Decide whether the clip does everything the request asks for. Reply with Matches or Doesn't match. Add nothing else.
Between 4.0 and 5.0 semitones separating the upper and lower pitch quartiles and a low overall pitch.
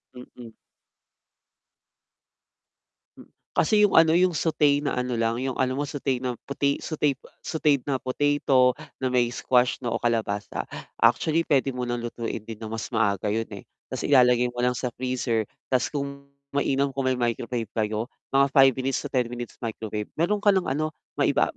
Doesn't match